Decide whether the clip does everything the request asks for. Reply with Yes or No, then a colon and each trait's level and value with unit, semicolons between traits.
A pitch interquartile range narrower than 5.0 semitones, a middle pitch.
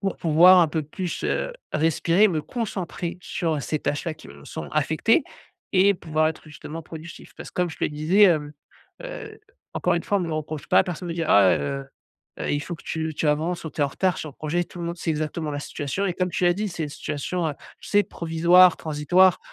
Yes: average, 2.8 semitones; medium, 165 Hz